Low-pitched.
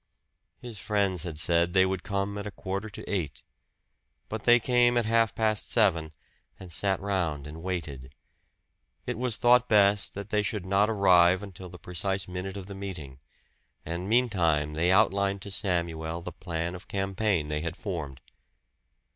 Yes: very low, 95 Hz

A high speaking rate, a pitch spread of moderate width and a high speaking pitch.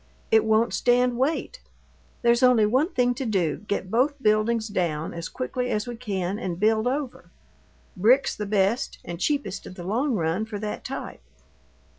No: average, 170 wpm; average, 4.3 semitones; high, 220 Hz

